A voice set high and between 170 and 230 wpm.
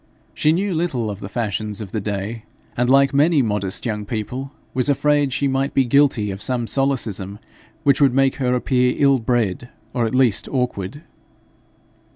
No: low, 125 Hz; average, 175 wpm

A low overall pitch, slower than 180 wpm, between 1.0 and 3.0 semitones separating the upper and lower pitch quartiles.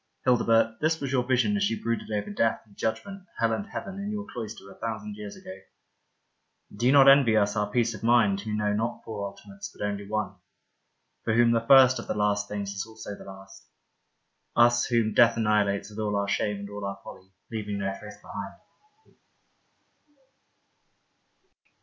No: low, 110 Hz; average, 185 wpm; narrow, 2.6 semitones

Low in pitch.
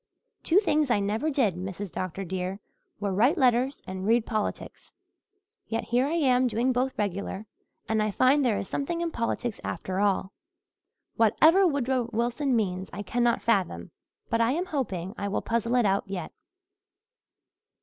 No: high, 230 Hz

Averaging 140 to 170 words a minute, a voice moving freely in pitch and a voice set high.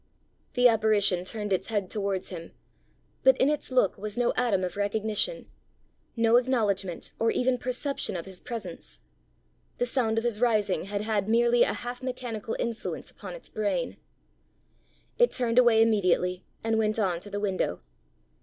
No: average, 160 wpm; average, 3.4 semitones; high, 220 Hz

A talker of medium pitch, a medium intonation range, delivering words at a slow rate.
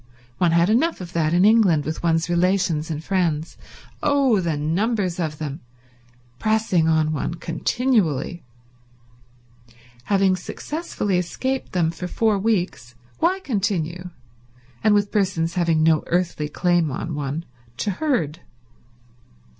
Yes: medium, 175 Hz; average, 4.4 semitones; slow, 120 wpm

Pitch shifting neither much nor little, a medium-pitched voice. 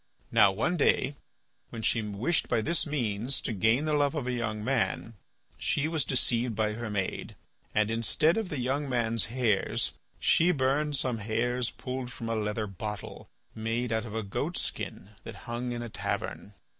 No: average, 3.5 semitones; low, 120 Hz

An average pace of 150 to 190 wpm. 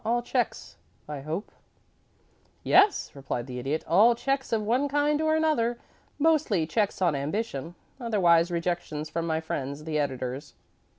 No: average, 140 wpm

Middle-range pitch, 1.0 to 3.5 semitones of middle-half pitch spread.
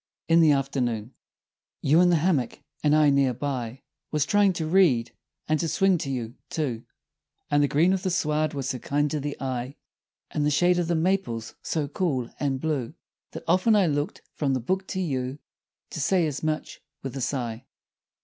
No: medium, 145 Hz; average, 4.2 semitones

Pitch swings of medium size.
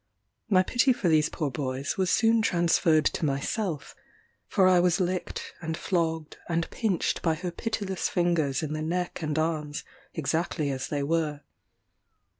Yes: average, 3.1 semitones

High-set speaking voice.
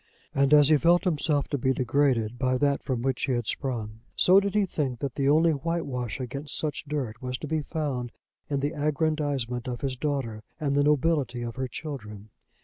No: medium, 140 Hz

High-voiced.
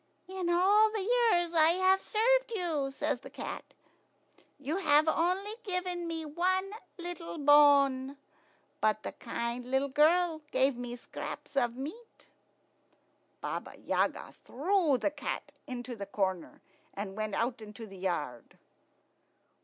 Yes: very high, 300 Hz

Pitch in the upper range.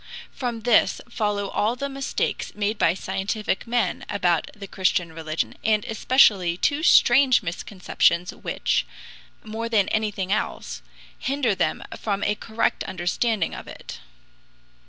Yes: high, 210 Hz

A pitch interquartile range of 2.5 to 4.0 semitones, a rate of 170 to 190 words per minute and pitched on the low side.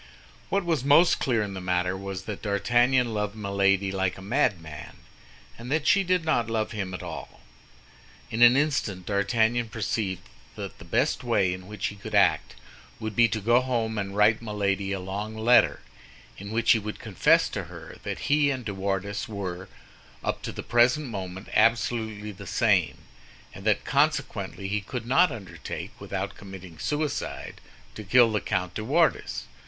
Yes: average, 3.6 semitones; average, 175 wpm; low, 105 Hz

